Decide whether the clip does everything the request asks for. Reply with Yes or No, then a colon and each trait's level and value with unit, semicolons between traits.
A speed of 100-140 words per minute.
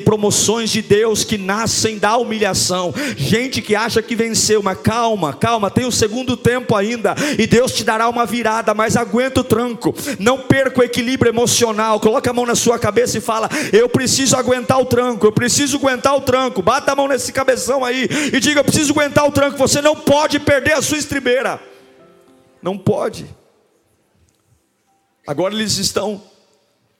No: average, 175 wpm